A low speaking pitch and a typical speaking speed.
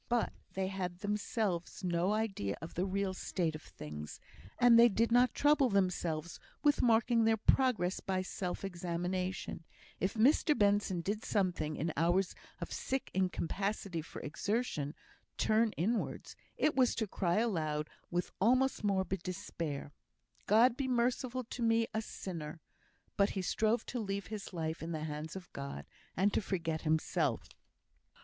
No: high, 195 Hz; average, 150 wpm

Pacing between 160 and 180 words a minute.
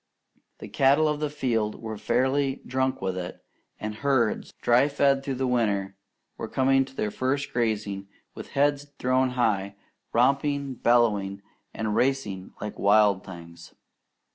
No: average, 140 wpm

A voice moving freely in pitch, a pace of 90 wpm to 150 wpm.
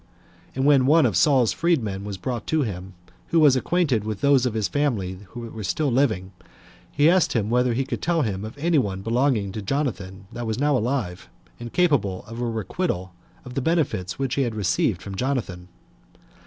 No: wide, 6.0 semitones; average, 200 wpm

